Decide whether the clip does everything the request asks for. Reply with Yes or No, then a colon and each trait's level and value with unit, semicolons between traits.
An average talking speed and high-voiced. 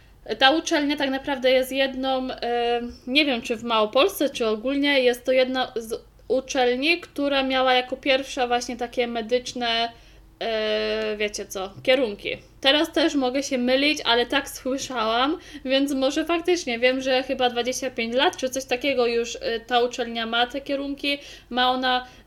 Yes: average, 150 wpm; very high, 255 Hz